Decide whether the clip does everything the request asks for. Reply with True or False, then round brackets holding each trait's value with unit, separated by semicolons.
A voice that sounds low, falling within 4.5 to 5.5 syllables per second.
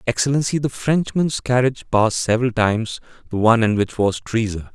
False (115 Hz; 6.1 syllables/s)